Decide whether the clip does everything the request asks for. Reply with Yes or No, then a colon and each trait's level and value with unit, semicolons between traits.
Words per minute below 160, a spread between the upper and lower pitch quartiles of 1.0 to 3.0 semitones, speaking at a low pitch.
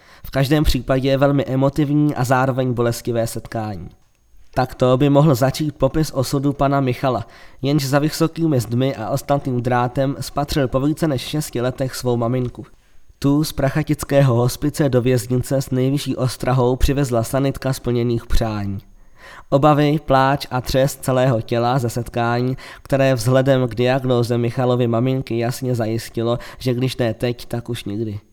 Yes: average, 150 wpm; narrow, 2.4 semitones; low, 130 Hz